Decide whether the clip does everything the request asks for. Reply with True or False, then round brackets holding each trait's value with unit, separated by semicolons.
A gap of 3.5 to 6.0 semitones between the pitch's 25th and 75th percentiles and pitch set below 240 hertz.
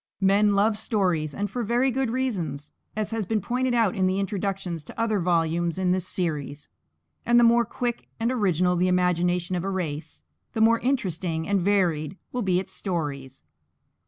True (4.5 semitones; 190 Hz)